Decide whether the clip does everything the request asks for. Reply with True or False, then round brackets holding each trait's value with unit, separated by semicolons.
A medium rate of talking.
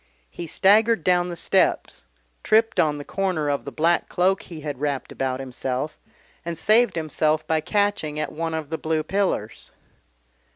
True (165 wpm)